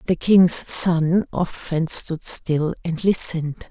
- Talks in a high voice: No, medium, 170 Hz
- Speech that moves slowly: Yes, slow, 130 wpm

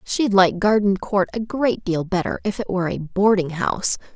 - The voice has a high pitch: Yes, high, 195 Hz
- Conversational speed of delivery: Yes, average, 190 wpm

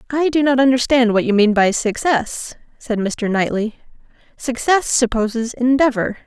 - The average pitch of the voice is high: Yes, high, 240 Hz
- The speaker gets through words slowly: No, average, 145 wpm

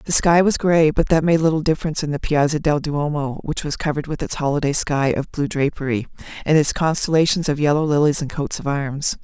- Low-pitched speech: No, medium, 150 Hz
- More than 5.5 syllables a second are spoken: Yes, 5.8 syllables/s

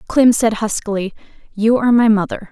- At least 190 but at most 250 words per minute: No, average, 165 wpm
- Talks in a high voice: Yes, high, 220 Hz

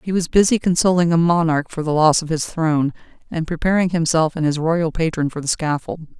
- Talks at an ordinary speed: No, fast, 215 wpm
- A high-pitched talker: No, medium, 165 Hz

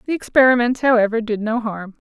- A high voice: Yes, high, 230 Hz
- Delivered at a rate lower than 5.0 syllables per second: No, 5.9 syllables/s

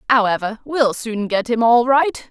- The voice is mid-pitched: No, high, 235 Hz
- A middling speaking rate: Yes, average, 180 wpm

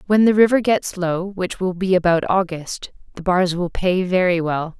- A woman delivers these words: Yes, female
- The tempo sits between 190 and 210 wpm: Yes, average, 200 wpm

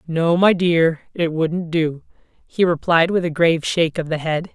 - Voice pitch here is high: No, medium, 165 Hz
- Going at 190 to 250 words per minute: Yes, average, 200 wpm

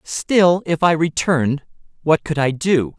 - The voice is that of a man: Yes, male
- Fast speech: No, average, 160 wpm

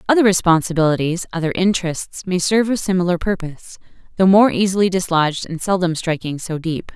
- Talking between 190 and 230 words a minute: No, average, 155 wpm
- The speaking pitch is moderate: Yes, medium, 180 Hz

